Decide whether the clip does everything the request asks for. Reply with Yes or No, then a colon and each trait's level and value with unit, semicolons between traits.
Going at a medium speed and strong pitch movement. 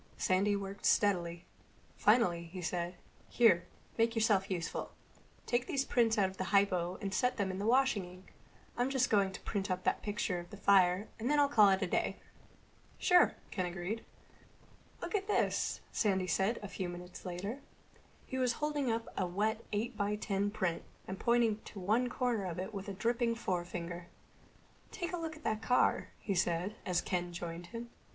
No: average, 185 wpm; average, 4.2 semitones